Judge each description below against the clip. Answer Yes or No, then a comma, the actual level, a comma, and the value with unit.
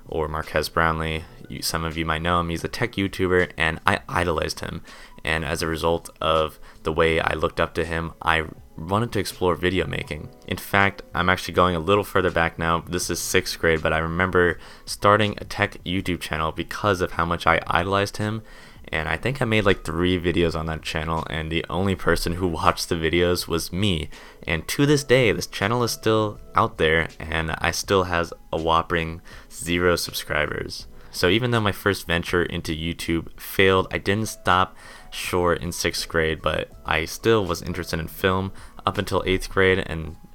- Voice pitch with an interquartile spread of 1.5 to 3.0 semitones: Yes, average, 2.7 semitones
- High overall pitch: No, very low, 85 Hz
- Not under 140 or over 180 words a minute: No, average, 195 wpm